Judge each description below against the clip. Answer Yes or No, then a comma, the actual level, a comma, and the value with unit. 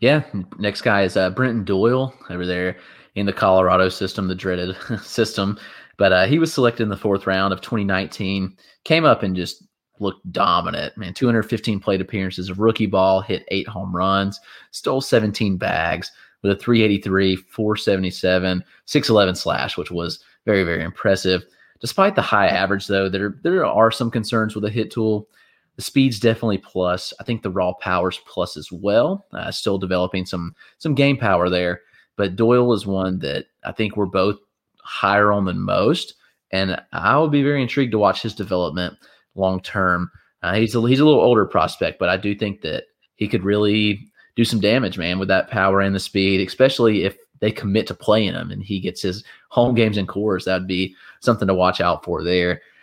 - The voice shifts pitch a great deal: No, average, 3.2 semitones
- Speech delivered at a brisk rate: No, average, 185 wpm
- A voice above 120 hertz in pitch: No, low, 100 Hz